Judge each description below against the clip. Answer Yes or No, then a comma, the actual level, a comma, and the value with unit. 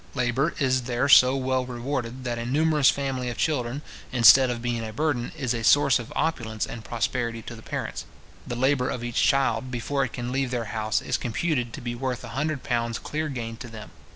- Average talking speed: No, fast, 210 wpm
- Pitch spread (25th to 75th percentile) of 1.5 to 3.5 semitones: Yes, narrow, 2.5 semitones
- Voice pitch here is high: No, low, 125 Hz